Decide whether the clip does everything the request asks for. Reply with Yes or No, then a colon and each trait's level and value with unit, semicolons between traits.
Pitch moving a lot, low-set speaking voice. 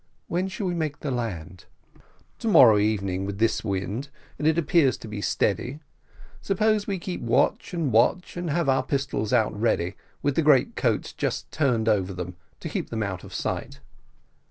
Yes: wide, 7.7 semitones; low, 125 Hz